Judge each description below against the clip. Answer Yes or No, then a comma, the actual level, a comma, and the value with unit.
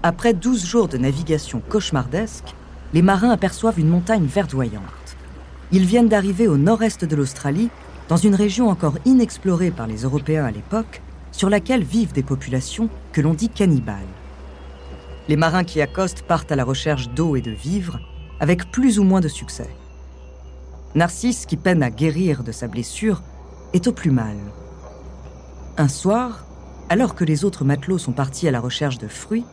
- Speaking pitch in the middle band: Yes, medium, 155 Hz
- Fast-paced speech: No, average, 165 wpm